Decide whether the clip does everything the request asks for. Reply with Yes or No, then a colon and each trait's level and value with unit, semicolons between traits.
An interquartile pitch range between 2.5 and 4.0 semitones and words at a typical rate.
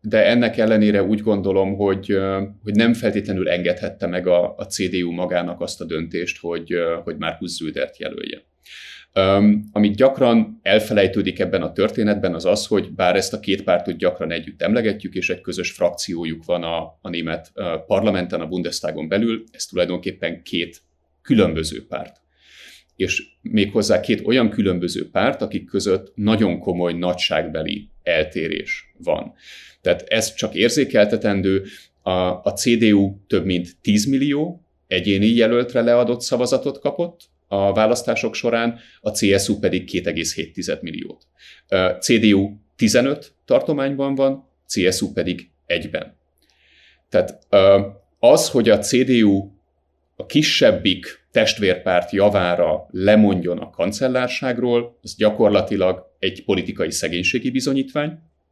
No: average, 5.0 semitones; average, 125 wpm